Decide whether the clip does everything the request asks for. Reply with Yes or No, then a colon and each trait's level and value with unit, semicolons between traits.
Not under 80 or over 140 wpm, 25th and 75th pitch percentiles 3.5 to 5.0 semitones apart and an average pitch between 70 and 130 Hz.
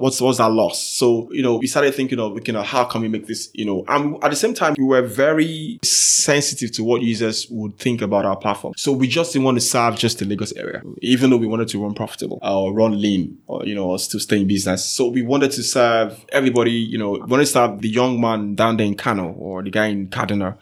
No: fast, 260 wpm; average, 3.8 semitones; low, 115 Hz